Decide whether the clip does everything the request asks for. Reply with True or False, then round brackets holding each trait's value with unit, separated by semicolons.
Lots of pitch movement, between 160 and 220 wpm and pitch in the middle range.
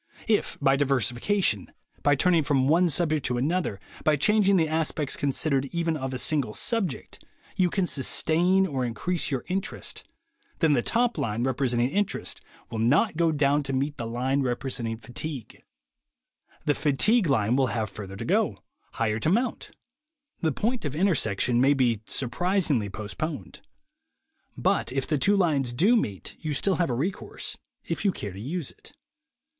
True (6.0 semitones; 165 wpm; 145 Hz)